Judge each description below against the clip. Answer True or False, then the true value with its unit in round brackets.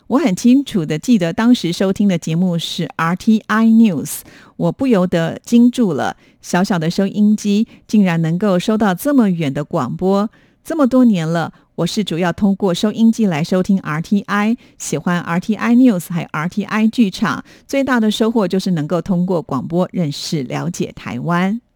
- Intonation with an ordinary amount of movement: True (4.6 semitones)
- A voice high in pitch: True (195 Hz)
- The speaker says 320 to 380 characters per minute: False (280 characters per minute)